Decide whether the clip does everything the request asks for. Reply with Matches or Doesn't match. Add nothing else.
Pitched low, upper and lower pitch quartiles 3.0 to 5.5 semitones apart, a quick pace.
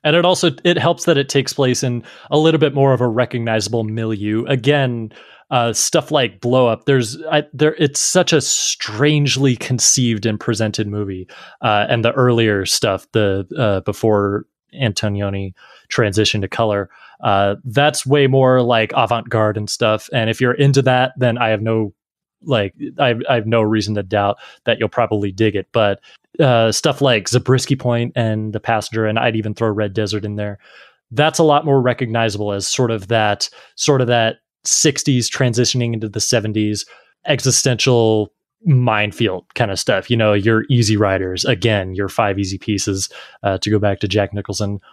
Doesn't match